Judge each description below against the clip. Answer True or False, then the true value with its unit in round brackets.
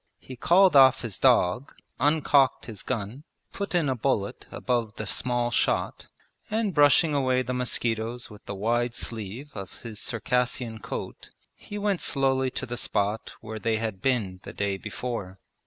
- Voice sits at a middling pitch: False (120 Hz)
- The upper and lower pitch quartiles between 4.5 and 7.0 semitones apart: False (3.6 semitones)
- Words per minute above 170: False (160 wpm)